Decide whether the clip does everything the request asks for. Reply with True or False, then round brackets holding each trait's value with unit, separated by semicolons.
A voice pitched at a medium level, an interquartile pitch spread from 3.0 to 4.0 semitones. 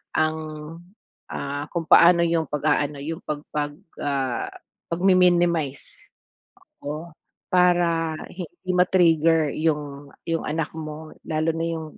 False (160 Hz; 2.4 semitones)